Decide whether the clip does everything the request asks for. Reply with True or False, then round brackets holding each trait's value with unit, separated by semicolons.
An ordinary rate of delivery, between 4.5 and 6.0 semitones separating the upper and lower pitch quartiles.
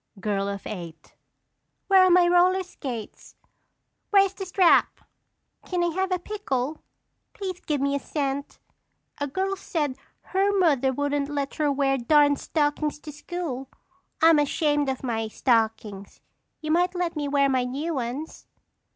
True (150 wpm; 5.0 semitones)